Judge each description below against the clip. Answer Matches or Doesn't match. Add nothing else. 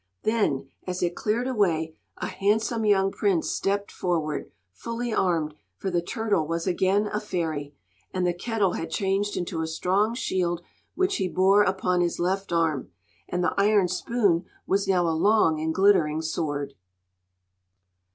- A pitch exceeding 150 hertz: Matches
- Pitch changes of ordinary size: Matches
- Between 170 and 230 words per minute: Doesn't match